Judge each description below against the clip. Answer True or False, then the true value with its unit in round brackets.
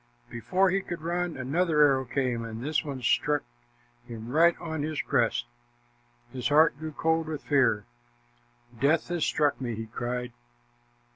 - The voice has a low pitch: False (145 Hz)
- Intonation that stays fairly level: False (4.7 semitones)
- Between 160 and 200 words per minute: False (150 wpm)